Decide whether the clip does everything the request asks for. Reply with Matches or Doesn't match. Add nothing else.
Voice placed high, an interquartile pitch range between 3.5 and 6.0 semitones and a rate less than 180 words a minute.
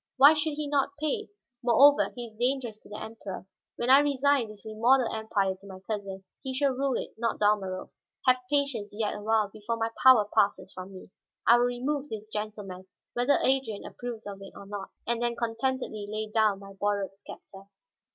Doesn't match